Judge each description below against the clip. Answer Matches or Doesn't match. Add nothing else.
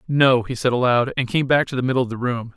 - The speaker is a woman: Doesn't match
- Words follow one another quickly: Matches